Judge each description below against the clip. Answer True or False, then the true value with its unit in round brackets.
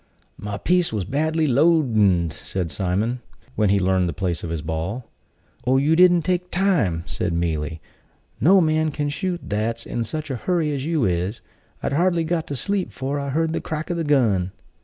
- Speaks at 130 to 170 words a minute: False (190 wpm)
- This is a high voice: False (135 Hz)